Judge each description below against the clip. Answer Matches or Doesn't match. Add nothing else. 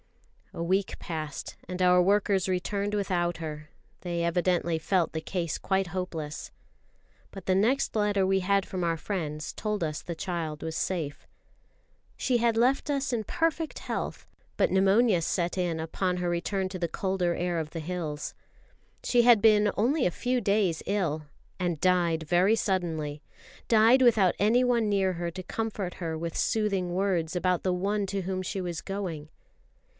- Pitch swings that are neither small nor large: Matches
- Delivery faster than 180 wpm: Doesn't match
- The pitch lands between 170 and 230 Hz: Matches